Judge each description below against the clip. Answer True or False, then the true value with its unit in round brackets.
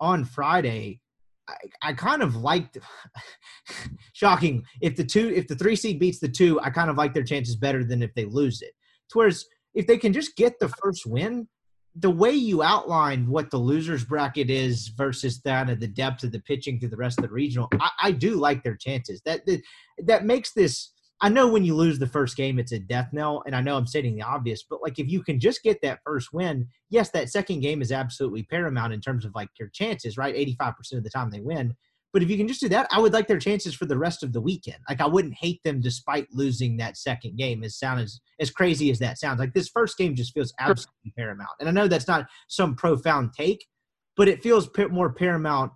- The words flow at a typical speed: False (235 wpm)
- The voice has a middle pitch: True (145 Hz)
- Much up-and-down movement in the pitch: True (6.5 semitones)